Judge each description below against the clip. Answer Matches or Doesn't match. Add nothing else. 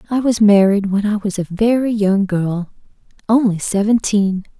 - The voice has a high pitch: Matches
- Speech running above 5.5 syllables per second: Doesn't match